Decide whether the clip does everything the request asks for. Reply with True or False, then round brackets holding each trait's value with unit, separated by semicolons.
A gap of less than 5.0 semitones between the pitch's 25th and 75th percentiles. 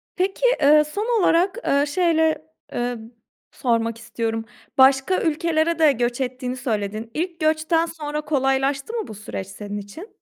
False (5.4 semitones)